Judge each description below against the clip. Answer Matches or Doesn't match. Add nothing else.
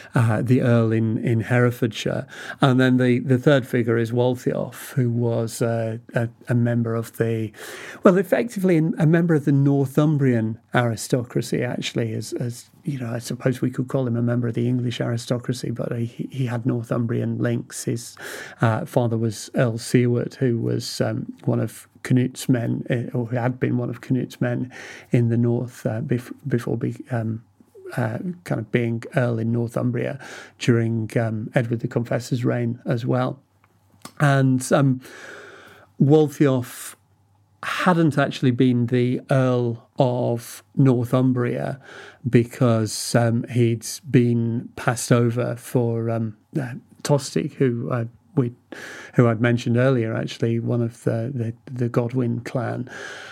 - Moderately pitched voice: Doesn't match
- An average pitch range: Doesn't match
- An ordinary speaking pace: Matches